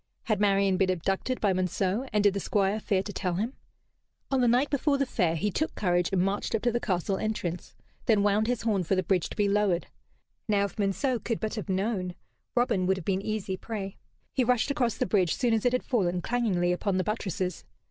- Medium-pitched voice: No, high, 200 Hz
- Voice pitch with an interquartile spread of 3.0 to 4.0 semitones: Yes, average, 3.5 semitones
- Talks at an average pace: No, fast, 225 wpm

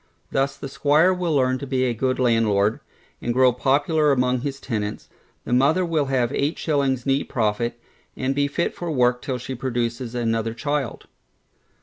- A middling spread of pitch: Yes, average, 3.0 semitones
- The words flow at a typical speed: Yes, average, 175 wpm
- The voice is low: Yes, low, 130 Hz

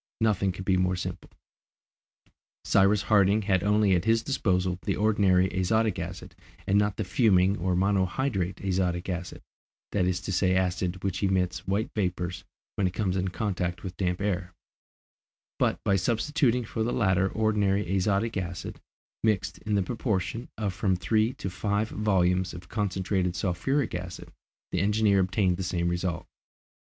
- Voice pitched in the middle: No, very low, 95 Hz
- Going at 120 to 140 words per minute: No, average, 155 wpm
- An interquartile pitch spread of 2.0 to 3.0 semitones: Yes, narrow, 2.4 semitones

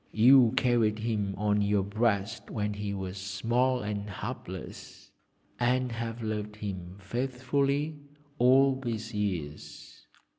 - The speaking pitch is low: Yes, low, 110 Hz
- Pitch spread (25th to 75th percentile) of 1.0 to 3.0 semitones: No, average, 3.5 semitones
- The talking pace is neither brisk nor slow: No, slow, 115 wpm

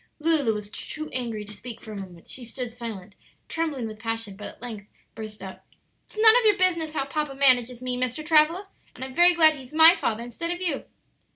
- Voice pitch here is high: Yes, very high, 255 Hz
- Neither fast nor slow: No, fast, 215 wpm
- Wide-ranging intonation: Yes, wide, 6.1 semitones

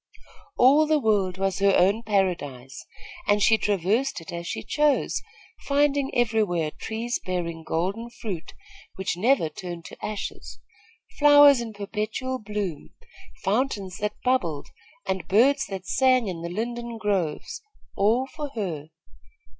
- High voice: Yes, high, 210 Hz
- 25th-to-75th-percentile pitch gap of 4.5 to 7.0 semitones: Yes, average, 5.2 semitones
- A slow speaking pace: Yes, slow, 130 wpm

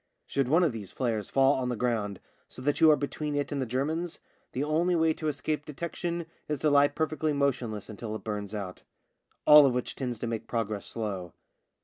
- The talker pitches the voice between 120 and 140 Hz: Yes, low, 135 Hz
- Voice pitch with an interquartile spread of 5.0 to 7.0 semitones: Yes, average, 5.3 semitones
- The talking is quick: Yes, fast, 210 wpm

